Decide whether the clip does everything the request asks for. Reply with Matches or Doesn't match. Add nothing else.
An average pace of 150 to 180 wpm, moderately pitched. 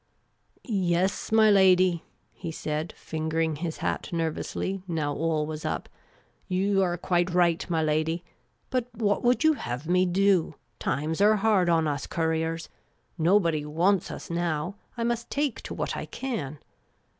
Matches